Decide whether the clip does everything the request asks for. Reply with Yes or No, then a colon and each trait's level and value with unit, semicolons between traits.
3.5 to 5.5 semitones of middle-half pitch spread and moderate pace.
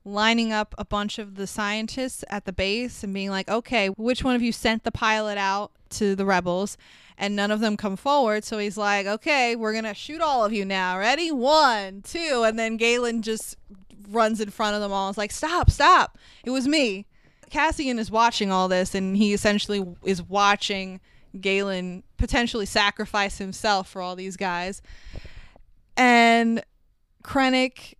No: average, 2.8 semitones; average, 175 wpm